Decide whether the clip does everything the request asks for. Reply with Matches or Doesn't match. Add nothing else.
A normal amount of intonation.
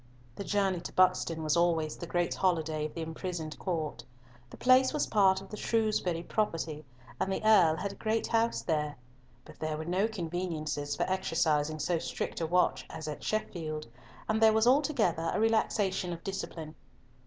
Matches